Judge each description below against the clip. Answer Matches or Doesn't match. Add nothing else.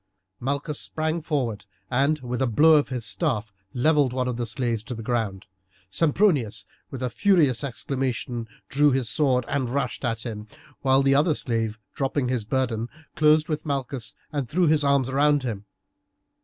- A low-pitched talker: Matches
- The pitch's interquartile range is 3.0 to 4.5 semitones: Matches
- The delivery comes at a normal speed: Matches